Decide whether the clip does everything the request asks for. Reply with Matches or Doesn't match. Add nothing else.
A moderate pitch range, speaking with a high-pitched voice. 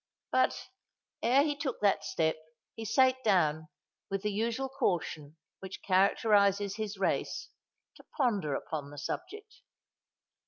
Doesn't match